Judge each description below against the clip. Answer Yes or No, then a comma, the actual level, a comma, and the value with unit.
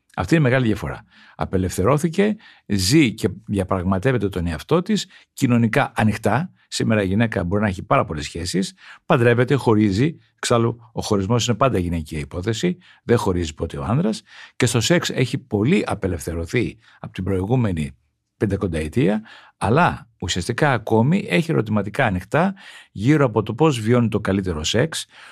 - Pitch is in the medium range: No, low, 110 Hz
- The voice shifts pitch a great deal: Yes, wide, 6.0 semitones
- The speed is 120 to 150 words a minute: Yes, average, 145 wpm